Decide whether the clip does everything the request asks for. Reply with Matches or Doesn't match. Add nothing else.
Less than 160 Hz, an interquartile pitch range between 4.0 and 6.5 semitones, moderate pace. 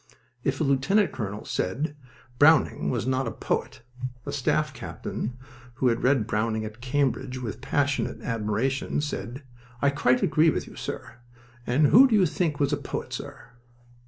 Doesn't match